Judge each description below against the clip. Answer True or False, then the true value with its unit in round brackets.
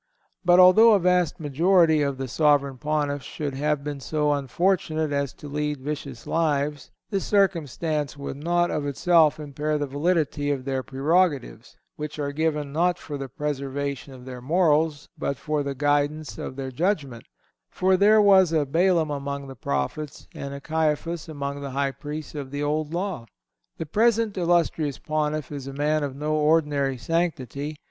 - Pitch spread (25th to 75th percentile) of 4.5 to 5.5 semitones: False (2.7 semitones)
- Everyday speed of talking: True (170 wpm)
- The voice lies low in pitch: False (150 Hz)